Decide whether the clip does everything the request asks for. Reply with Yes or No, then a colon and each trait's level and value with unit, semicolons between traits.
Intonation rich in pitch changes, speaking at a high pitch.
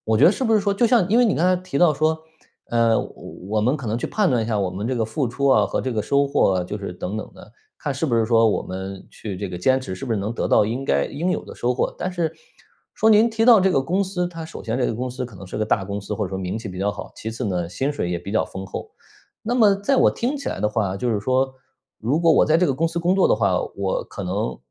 No: wide, 8.7 semitones; low, 125 Hz